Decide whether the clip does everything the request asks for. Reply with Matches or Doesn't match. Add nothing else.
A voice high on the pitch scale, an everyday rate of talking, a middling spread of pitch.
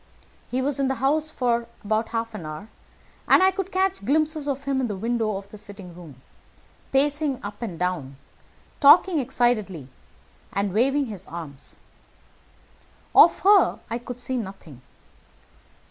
Doesn't match